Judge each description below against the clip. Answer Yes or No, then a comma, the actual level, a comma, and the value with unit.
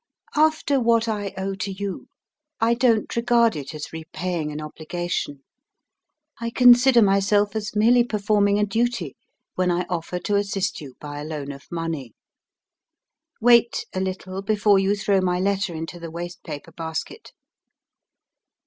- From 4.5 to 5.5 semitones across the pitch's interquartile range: Yes, average, 4.8 semitones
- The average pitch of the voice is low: No, high, 195 Hz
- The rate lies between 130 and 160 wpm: Yes, average, 150 wpm